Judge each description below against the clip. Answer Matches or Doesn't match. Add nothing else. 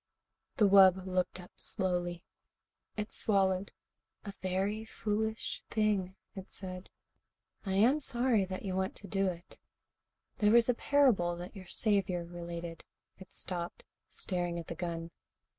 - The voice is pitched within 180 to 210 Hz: Matches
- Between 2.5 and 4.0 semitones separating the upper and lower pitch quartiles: Matches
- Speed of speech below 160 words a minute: Matches